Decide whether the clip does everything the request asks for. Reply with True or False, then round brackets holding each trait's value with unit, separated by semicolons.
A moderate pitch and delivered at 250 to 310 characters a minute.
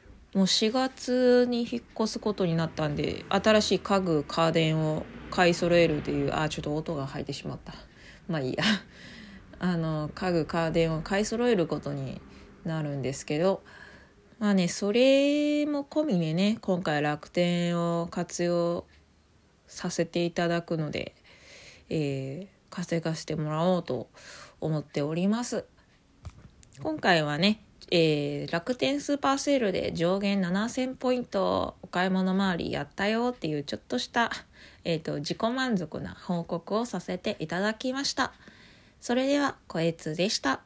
True (175 Hz; 280 characters per minute)